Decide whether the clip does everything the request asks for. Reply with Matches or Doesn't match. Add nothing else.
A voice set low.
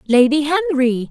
Doesn't match